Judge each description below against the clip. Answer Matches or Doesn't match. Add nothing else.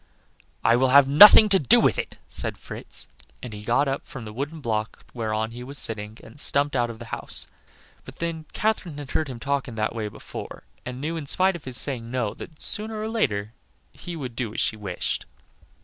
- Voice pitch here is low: Matches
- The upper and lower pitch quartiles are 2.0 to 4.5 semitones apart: Doesn't match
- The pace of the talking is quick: Matches